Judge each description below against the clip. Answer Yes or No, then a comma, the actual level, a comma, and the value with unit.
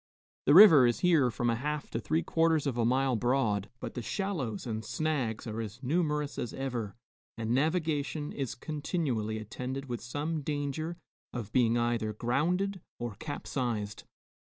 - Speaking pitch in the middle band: No, low, 130 Hz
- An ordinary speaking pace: Yes, average, 160 wpm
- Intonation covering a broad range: No, average, 4.8 semitones